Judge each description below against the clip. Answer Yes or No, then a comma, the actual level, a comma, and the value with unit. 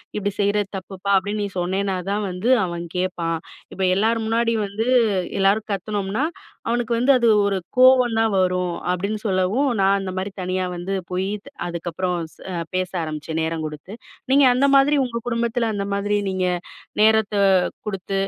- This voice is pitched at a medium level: No, high, 200 Hz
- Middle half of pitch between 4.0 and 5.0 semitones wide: No, average, 3.4 semitones